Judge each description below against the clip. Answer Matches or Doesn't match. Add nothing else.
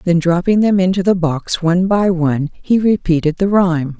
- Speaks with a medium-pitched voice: Matches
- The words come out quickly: Doesn't match